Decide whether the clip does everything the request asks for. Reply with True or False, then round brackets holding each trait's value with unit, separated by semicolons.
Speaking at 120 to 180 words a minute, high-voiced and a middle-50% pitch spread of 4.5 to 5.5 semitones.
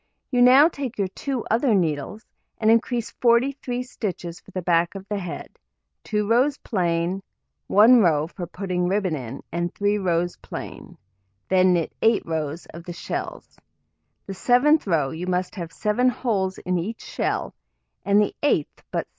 True (165 wpm; 195 Hz; 5.2 semitones)